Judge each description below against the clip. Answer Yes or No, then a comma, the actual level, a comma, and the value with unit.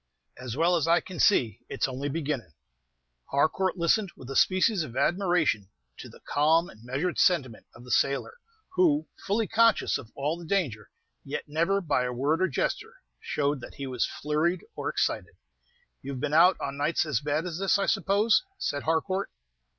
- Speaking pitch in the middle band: Yes, medium, 155 Hz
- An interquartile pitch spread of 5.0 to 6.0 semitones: Yes, average, 5.3 semitones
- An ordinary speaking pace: Yes, average, 180 wpm